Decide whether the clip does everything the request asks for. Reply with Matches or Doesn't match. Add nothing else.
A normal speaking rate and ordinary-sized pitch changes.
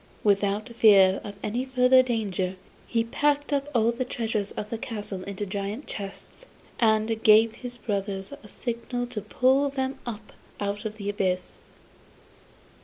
Matches